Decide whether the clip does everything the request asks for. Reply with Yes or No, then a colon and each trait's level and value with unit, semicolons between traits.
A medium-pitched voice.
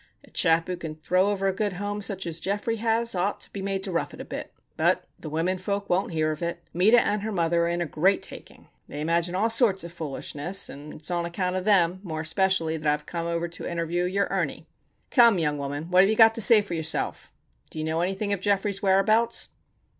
Yes: medium, 180 Hz